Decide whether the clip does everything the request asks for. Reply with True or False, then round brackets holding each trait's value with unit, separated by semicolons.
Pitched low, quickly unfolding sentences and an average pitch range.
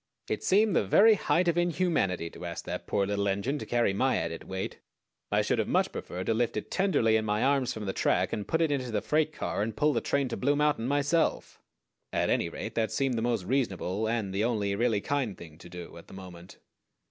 False (115 Hz; 235 wpm; 6.5 semitones)